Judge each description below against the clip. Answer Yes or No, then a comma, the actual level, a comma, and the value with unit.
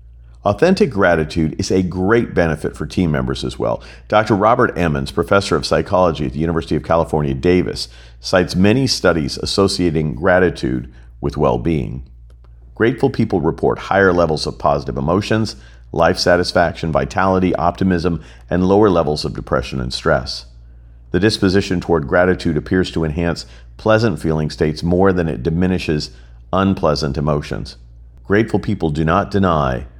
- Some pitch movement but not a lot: No, wide, 6.0 semitones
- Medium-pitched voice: No, very low, 80 Hz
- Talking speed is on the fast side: No, average, 140 wpm